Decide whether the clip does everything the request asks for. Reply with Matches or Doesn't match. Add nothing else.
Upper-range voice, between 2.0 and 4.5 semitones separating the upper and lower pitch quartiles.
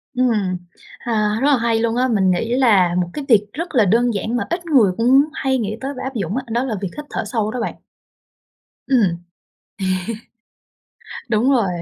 Matches